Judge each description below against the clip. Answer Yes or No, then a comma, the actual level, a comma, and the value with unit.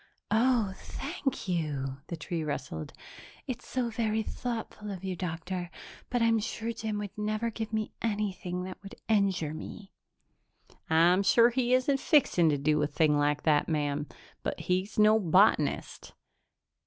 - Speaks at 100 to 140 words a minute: No, average, 150 wpm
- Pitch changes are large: Yes, wide, 5.7 semitones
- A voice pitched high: Yes, high, 195 Hz